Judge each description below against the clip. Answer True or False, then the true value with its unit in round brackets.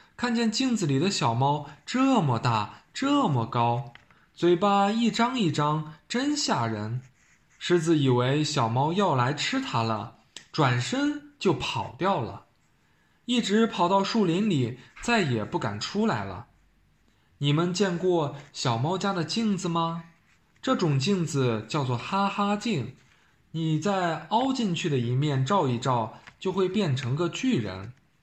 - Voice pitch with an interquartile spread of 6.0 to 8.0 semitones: True (7.3 semitones)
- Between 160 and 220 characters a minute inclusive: True (195 characters per minute)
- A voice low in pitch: False (165 Hz)